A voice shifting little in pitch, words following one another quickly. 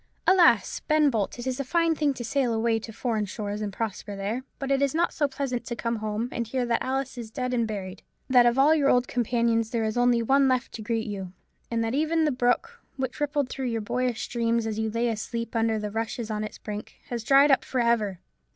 No: average, 3.2 semitones; fast, 240 wpm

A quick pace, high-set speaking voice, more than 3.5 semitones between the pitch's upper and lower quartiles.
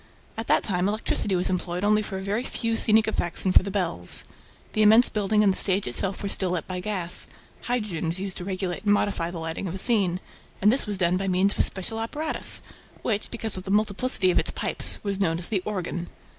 No: fast, 235 wpm; high, 195 Hz; average, 2.8 semitones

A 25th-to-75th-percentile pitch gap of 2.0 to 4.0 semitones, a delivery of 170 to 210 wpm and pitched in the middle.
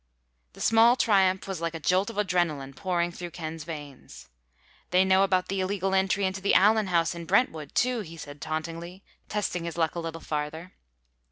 Yes: average, 2.8 semitones; average, 185 wpm; medium, 180 Hz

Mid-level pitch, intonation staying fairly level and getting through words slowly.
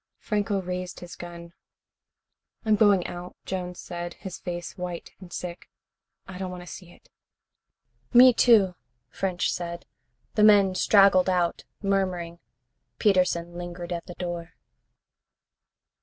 Yes: medium, 180 Hz; narrow, 1.9 semitones; slow, 125 wpm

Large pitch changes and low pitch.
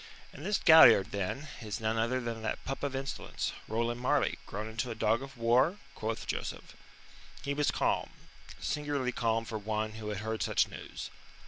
No: average, 3.6 semitones; low, 115 Hz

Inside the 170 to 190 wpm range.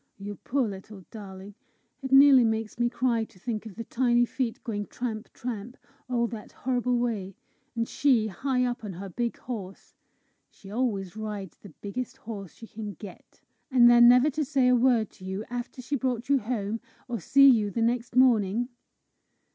Yes: average, 180 wpm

